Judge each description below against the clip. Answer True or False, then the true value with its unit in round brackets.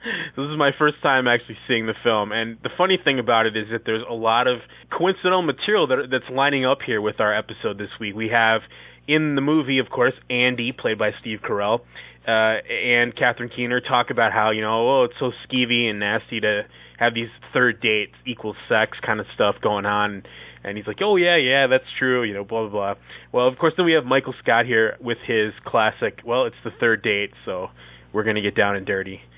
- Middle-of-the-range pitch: False (115 Hz)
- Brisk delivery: True (225 wpm)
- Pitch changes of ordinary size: True (3.4 semitones)